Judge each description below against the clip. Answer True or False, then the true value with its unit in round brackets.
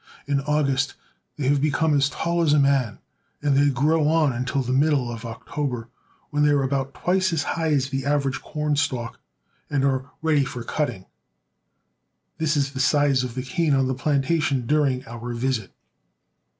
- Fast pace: False (175 wpm)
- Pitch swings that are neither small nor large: False (2.3 semitones)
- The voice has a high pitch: False (140 Hz)